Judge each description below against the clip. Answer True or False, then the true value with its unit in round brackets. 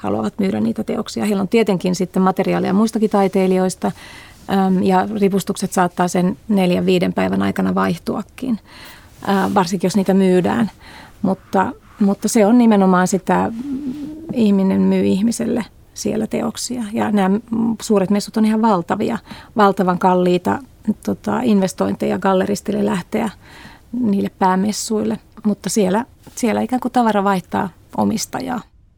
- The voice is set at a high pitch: True (200 Hz)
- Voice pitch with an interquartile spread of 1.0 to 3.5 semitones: True (2.8 semitones)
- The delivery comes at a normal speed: True (120 wpm)